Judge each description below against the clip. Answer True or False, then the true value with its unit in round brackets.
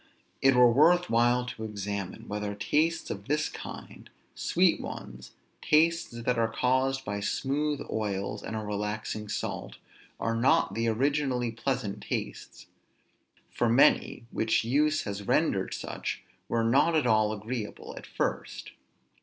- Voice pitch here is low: True (115 Hz)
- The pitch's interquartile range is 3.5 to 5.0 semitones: True (4.2 semitones)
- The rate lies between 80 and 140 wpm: True (135 wpm)